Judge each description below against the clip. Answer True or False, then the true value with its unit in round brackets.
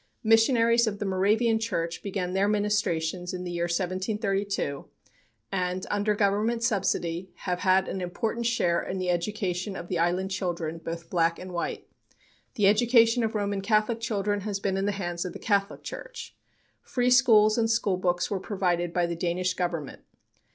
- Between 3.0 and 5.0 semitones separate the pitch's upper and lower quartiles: True (3.3 semitones)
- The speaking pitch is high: True (195 Hz)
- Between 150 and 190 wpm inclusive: True (165 wpm)